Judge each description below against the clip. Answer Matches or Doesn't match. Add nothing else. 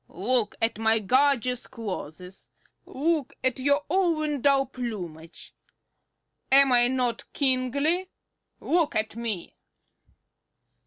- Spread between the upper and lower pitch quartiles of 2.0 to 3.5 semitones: Doesn't match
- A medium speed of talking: Doesn't match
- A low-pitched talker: Doesn't match